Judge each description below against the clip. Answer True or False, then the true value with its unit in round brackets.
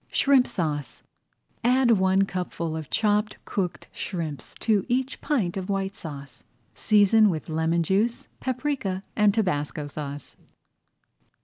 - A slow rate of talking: True (120 wpm)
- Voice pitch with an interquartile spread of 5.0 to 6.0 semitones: True (5.6 semitones)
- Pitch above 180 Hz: True (190 Hz)